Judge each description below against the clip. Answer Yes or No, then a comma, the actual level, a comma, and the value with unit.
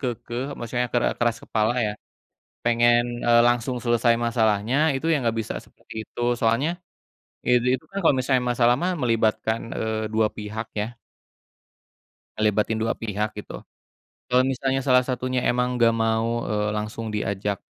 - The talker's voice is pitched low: Yes, low, 115 Hz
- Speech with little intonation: Yes, narrow, 2.2 semitones